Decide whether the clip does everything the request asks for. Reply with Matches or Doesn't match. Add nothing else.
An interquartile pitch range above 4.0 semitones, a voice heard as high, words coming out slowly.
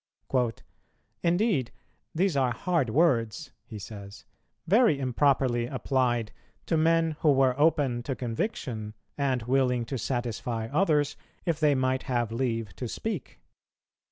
Doesn't match